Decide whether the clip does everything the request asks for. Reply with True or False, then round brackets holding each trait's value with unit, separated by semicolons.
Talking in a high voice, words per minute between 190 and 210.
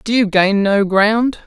True (210 Hz; 205 wpm)